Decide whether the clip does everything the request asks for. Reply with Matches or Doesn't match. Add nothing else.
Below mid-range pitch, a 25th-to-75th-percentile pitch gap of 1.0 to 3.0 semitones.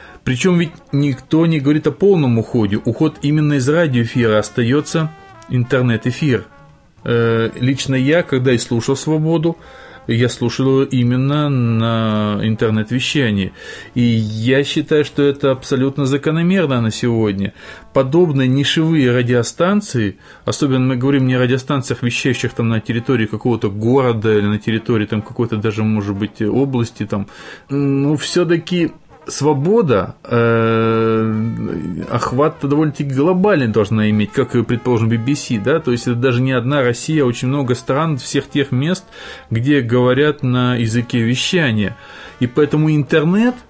Doesn't match